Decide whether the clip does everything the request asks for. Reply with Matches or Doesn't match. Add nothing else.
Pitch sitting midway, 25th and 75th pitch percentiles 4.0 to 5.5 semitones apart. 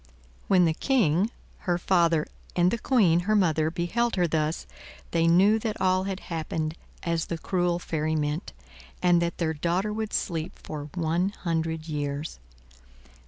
Doesn't match